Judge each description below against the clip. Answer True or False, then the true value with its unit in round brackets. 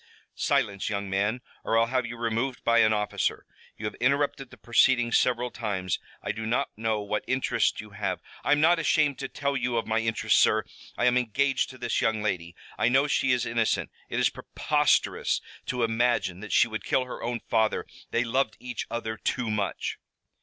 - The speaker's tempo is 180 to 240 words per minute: True (200 wpm)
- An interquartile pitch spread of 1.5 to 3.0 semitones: True (2.7 semitones)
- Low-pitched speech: True (115 Hz)